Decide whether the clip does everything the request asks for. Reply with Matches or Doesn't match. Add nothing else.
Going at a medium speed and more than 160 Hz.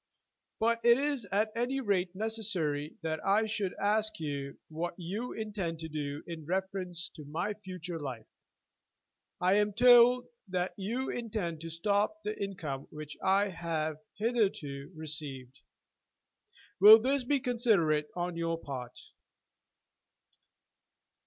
Doesn't match